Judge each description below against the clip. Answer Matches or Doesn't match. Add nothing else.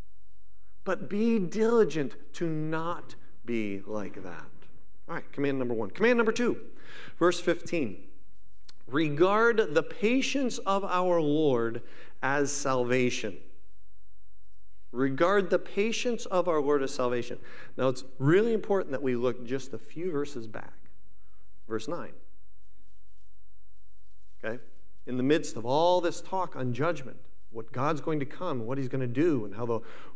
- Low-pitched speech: Matches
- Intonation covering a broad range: Matches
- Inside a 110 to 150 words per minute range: Matches